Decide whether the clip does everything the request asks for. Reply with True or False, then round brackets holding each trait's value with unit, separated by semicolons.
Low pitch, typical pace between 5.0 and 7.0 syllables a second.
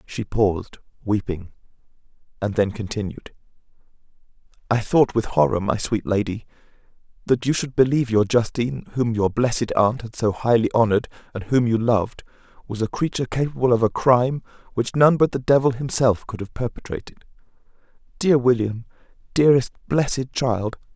True (120 Hz; 5.5 syllables/s)